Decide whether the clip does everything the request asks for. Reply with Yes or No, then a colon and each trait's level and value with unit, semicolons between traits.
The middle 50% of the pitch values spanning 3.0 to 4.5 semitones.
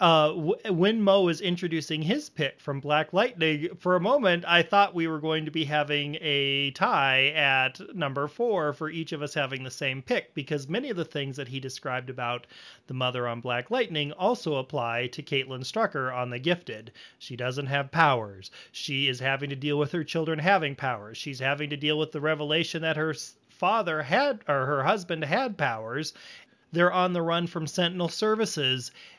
Yes: average, 3.9 semitones